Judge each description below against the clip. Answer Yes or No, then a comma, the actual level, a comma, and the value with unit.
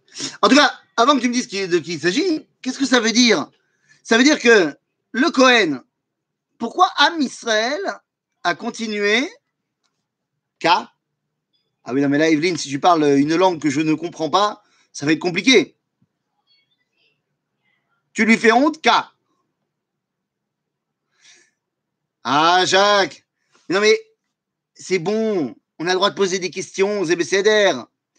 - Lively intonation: Yes, wide, 6.4 semitones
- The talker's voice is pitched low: No, high, 215 Hz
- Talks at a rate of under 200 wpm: Yes, average, 150 wpm